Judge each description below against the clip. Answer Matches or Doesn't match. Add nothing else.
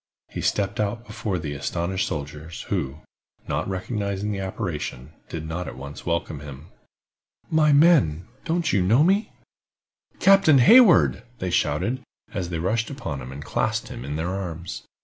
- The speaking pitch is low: Matches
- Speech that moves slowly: Doesn't match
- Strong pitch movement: Matches